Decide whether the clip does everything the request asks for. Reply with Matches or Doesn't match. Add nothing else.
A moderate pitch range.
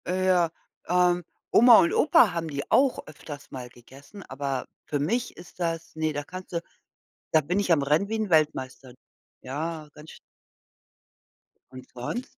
Matches